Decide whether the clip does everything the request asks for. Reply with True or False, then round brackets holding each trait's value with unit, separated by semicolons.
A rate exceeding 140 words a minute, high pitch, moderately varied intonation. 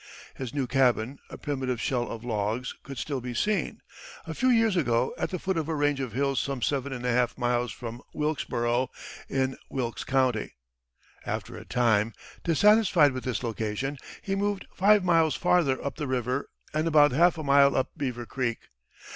False (180 wpm; 135 Hz; 4.2 semitones)